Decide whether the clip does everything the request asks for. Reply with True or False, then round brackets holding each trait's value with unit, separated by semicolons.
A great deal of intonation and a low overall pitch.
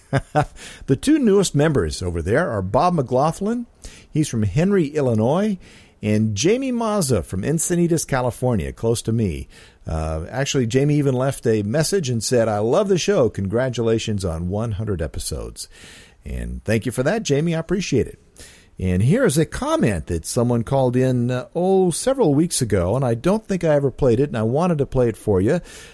True (7.3 semitones; 130 Hz)